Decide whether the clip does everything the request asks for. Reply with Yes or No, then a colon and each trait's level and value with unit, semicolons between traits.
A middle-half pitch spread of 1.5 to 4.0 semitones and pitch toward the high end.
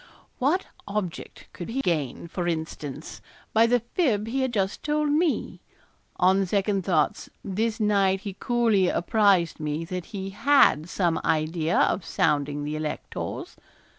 No: wide, 5.5 semitones; high, 195 Hz